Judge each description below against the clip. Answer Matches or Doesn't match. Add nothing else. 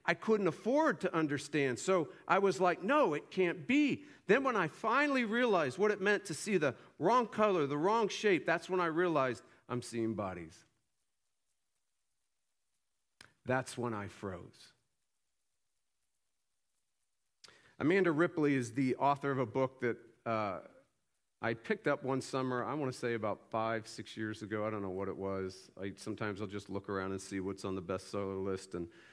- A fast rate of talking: Doesn't match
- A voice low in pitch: Matches